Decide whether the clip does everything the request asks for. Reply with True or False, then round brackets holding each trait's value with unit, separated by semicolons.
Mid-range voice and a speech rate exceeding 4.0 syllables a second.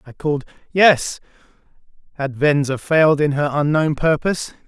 True (150 Hz; 5.1 syllables/s)